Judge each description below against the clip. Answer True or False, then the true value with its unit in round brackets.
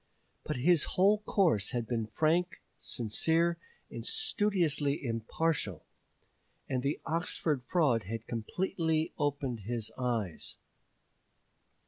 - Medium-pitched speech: True (145 Hz)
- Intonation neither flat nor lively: False (6.6 semitones)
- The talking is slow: True (100 wpm)